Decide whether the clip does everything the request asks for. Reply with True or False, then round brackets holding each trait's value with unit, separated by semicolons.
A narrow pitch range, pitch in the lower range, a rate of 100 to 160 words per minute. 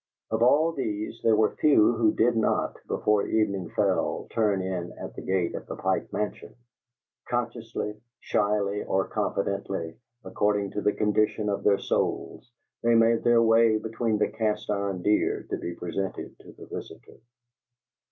True (2.3 semitones; 105 Hz; 155 wpm)